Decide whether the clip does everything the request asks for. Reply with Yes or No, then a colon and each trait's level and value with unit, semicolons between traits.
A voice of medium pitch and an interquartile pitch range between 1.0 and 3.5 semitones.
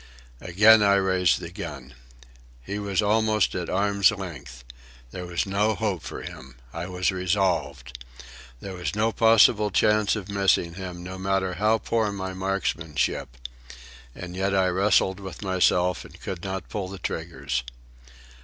No: very low, 95 Hz; narrow, 2.4 semitones